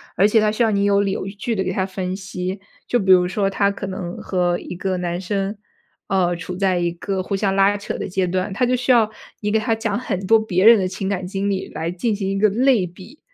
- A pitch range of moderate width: No, narrow, 2.2 semitones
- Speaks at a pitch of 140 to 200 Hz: Yes, high, 195 Hz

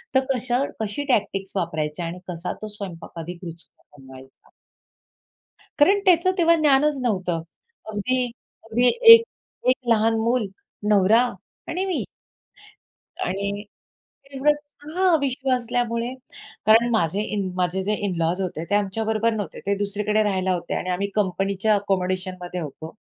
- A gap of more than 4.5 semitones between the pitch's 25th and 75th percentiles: Yes, average, 5.2 semitones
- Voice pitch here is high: Yes, high, 205 Hz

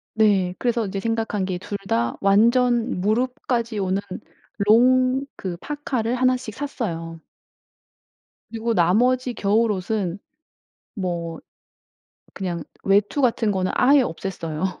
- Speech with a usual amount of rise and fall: Yes, average, 4.6 semitones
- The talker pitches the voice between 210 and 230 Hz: Yes, high, 215 Hz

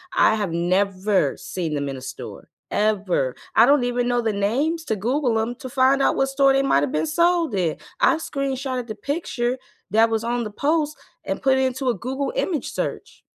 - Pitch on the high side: Yes, high, 245 Hz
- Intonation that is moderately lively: Yes, average, 5.0 semitones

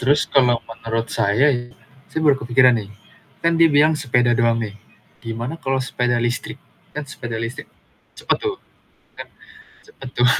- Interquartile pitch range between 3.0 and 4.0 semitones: Yes, average, 3.6 semitones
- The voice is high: No, low, 125 Hz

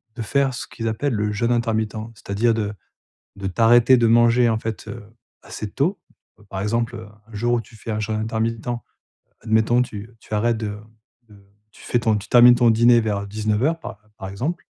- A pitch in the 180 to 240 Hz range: No, low, 115 Hz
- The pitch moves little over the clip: Yes, narrow, 2.0 semitones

